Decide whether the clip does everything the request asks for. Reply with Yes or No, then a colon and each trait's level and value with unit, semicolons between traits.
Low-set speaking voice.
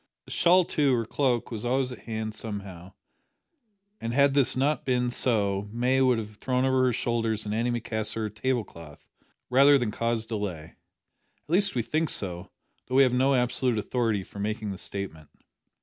Yes: low, 115 Hz